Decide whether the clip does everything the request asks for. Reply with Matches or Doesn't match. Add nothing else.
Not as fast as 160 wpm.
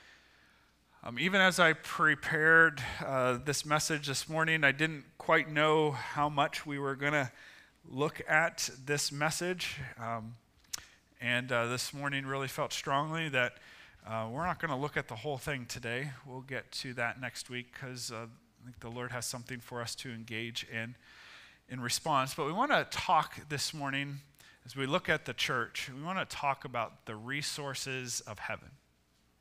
Doesn't match